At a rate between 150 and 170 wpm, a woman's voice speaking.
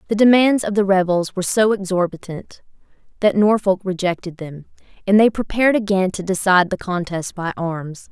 Yes: average, 165 wpm; female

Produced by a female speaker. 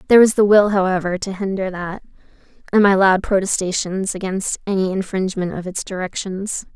Yes: female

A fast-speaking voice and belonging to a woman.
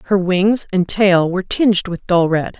Yes: fast, 210 wpm; female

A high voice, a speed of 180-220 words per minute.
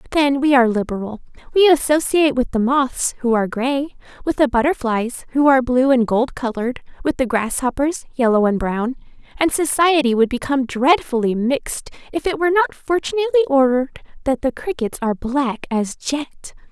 No: very high, 265 Hz; average, 165 wpm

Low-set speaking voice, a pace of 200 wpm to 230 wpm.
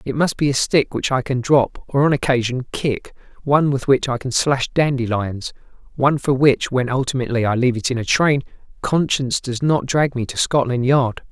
Yes: low, 130 Hz; fast, 205 wpm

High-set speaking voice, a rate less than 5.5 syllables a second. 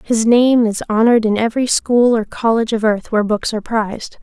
No: high, 225 Hz; 5.9 syllables/s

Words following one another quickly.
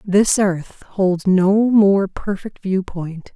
No: average, 145 wpm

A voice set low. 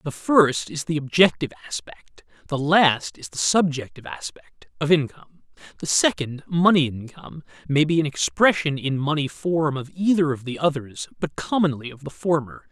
No: medium, 150 Hz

